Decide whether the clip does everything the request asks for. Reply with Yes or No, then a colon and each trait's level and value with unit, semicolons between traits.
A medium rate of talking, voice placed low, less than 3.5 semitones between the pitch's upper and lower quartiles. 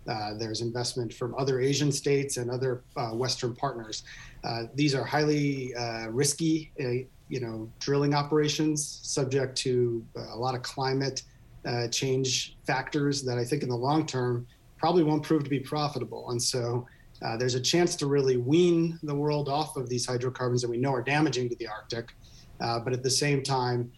Yes: average, 185 wpm; low, 130 Hz; average, 2.9 semitones